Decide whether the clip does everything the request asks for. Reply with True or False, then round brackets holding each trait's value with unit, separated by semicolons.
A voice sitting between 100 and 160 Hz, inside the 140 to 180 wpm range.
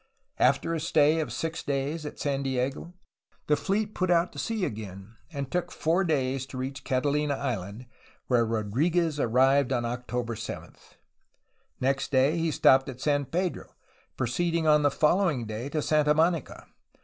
True (140 Hz; 160 wpm)